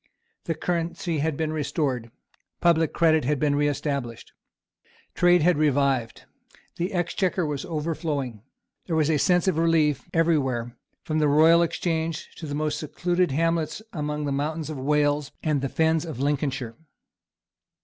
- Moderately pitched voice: Yes, medium, 155 Hz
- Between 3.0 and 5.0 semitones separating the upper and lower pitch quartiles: No, narrow, 2.6 semitones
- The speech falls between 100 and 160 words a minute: Yes, average, 150 wpm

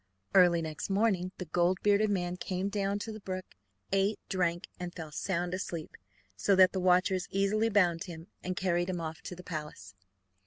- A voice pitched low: No, medium, 185 Hz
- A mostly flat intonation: Yes, narrow, 2.2 semitones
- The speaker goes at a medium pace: Yes, average, 185 wpm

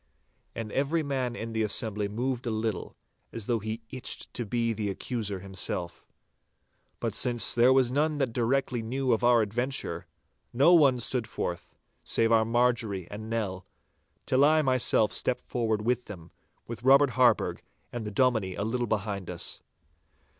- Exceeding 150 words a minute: Yes, average, 160 wpm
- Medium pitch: No, low, 115 Hz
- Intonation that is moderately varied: Yes, average, 3.0 semitones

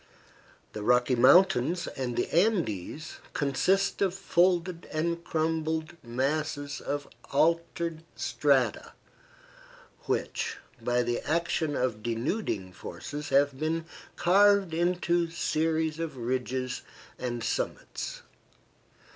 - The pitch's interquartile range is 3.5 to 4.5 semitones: No, average, 4.9 semitones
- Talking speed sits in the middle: No, slow, 95 wpm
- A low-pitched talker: No, medium, 155 Hz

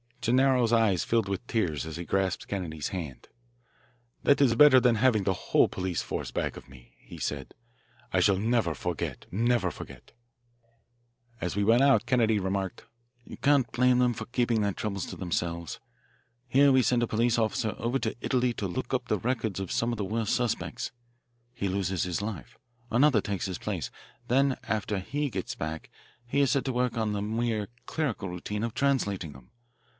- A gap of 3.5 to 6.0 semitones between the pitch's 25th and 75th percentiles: Yes, average, 4.5 semitones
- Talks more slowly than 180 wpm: No, average, 185 wpm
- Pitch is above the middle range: No, low, 110 Hz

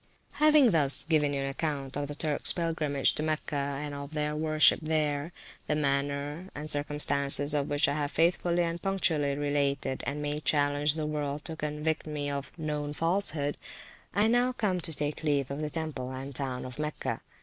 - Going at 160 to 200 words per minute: Yes, average, 185 wpm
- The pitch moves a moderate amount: No, narrow, 1.9 semitones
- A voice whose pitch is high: No, medium, 150 Hz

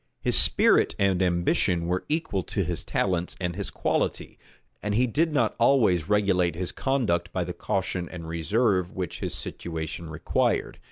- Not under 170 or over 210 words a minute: No, average, 160 wpm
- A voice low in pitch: Yes, very low, 90 Hz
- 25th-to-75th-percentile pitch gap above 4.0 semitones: No, average, 3.4 semitones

